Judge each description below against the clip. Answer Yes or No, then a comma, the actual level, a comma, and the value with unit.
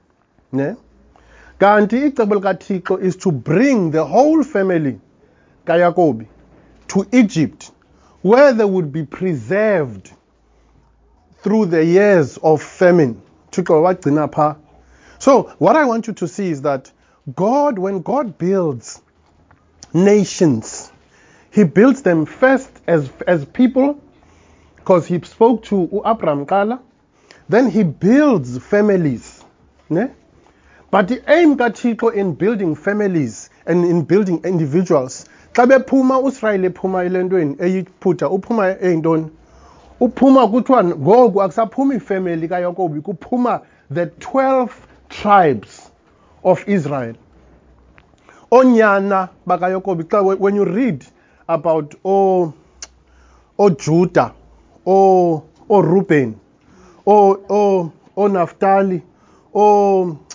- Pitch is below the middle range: No, medium, 185 Hz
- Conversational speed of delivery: No, slow, 95 wpm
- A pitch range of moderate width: Yes, average, 4.9 semitones